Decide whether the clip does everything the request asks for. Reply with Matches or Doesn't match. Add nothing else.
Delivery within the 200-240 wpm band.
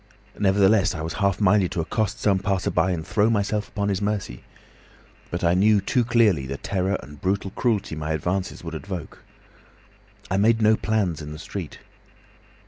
Doesn't match